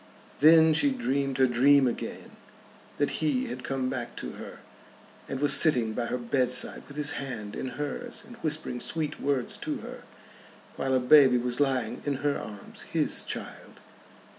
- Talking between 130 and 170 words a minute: Yes, average, 165 wpm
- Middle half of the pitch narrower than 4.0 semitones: Yes, average, 2.8 semitones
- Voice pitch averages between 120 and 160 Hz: Yes, low, 135 Hz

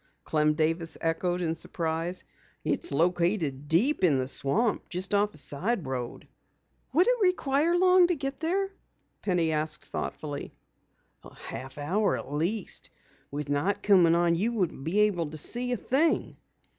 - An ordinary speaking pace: Yes, average, 155 wpm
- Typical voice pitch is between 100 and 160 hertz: No, medium, 175 Hz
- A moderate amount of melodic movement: No, wide, 7.4 semitones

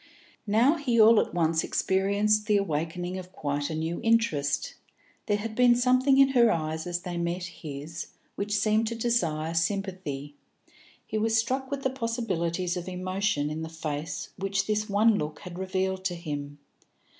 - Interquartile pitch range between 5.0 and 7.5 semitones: Yes, wide, 5.4 semitones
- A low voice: No, high, 190 Hz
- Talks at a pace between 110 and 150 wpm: No, average, 170 wpm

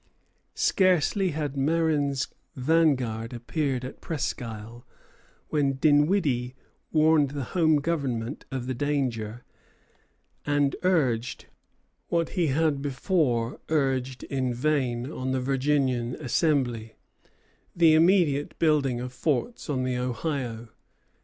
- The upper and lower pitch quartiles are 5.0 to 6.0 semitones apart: No, average, 3.8 semitones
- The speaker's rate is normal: No, slow, 105 wpm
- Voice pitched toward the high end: No, medium, 140 Hz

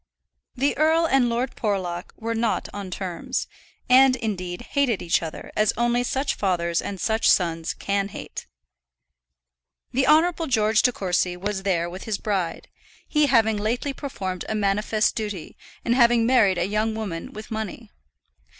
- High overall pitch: Yes, high, 215 Hz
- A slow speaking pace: No, average, 155 wpm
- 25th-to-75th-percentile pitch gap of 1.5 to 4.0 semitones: No, average, 4.4 semitones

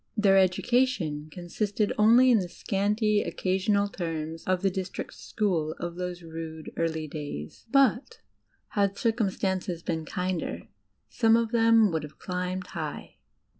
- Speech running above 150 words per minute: No, slow, 135 wpm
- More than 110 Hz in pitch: Yes, medium, 185 Hz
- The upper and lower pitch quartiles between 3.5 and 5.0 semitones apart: Yes, average, 4.4 semitones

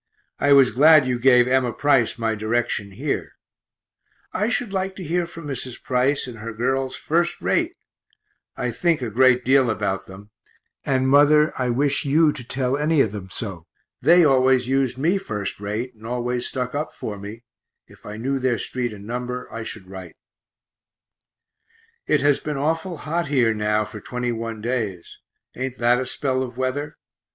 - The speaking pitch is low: Yes, low, 130 Hz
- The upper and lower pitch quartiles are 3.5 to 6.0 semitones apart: Yes, average, 4.0 semitones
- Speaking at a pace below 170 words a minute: No, average, 175 wpm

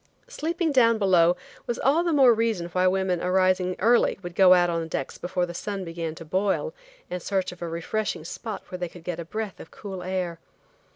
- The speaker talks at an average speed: No, fast, 210 wpm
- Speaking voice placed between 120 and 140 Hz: No, medium, 185 Hz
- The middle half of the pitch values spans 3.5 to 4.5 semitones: Yes, average, 3.8 semitones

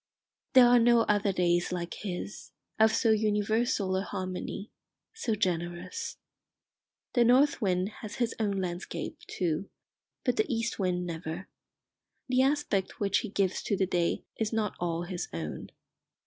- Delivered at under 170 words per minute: Yes, average, 150 wpm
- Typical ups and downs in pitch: Yes, average, 4.1 semitones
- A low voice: No, high, 200 Hz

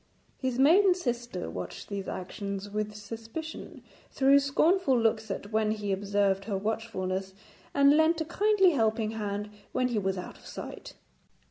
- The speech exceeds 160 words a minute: No, average, 150 wpm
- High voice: Yes, high, 220 Hz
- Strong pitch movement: Yes, wide, 5.7 semitones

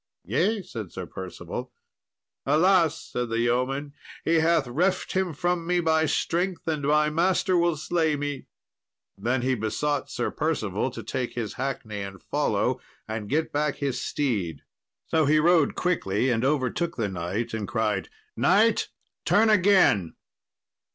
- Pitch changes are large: Yes, wide, 6.5 semitones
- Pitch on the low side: No, medium, 145 Hz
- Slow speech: No, average, 145 wpm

